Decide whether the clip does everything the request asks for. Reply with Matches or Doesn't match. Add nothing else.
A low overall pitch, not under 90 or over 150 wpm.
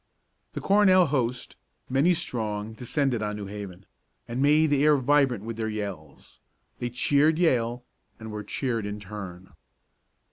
Matches